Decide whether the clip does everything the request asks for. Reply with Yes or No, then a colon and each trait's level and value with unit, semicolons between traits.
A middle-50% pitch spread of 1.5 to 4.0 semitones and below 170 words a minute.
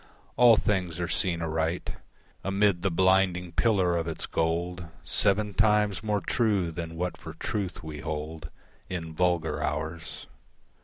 Yes: average, 3.2 semitones; average, 140 wpm